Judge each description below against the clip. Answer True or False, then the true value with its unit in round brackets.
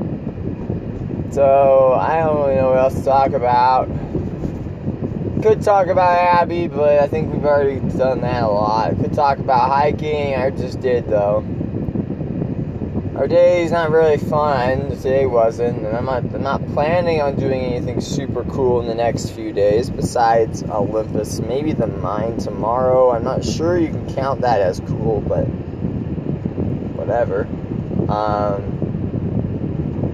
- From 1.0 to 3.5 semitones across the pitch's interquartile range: False (4.4 semitones)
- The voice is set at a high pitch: False (130 Hz)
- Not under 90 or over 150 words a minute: True (145 wpm)